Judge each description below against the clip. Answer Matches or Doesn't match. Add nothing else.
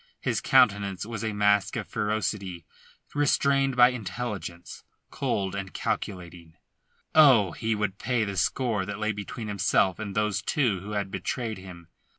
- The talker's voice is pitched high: Doesn't match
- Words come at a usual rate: Matches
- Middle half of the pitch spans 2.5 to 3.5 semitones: Matches